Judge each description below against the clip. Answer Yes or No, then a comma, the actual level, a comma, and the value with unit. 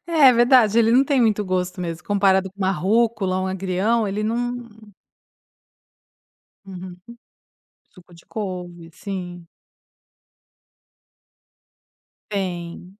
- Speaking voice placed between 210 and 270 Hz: No, high, 195 Hz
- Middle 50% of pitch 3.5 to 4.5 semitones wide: Yes, average, 3.9 semitones